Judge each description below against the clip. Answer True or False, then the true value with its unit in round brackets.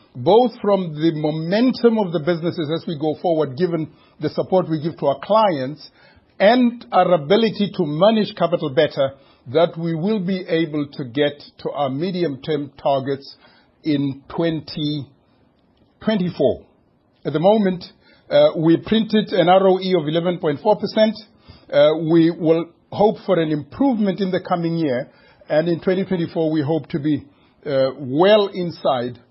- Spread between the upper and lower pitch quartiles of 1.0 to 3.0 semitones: False (4.3 semitones)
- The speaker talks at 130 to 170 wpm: True (145 wpm)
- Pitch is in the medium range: True (170 Hz)